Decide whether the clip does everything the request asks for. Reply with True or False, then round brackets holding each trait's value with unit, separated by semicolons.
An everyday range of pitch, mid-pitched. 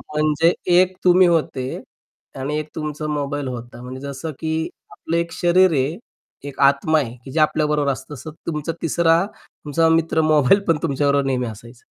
True (3.0 semitones; 150 Hz)